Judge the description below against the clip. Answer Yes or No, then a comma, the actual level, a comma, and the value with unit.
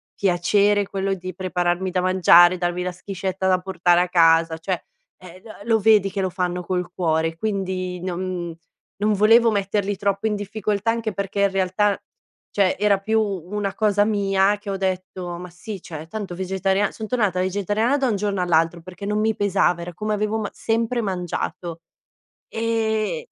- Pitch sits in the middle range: No, high, 195 Hz